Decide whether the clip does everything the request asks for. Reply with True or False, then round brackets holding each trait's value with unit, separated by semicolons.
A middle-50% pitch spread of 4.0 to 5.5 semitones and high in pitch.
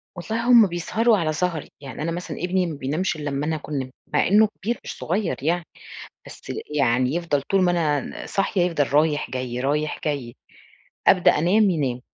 False (4.3 semitones; 160 Hz)